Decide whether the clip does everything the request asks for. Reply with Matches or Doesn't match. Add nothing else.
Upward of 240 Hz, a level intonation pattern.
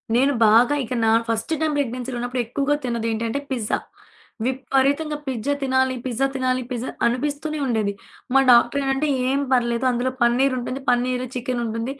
Matches